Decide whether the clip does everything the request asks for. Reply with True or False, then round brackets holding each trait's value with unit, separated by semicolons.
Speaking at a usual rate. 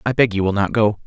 False (340 wpm)